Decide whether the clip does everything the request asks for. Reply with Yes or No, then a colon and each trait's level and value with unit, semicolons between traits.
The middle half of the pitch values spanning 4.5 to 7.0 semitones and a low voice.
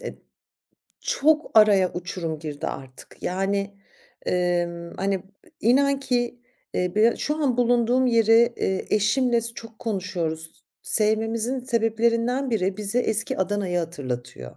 No: average, 4.9 semitones; high, 215 Hz